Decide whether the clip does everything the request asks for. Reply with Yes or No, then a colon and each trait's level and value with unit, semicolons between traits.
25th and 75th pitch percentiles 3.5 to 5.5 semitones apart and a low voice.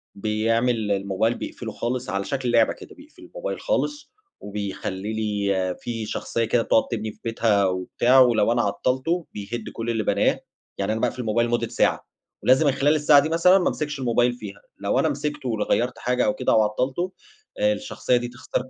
Yes: average, 3.8 semitones; low, 120 Hz